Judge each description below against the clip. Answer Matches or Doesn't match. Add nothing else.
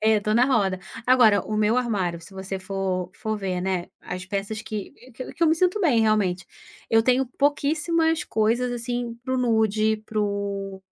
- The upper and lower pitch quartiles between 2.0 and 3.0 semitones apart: Doesn't match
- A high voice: Matches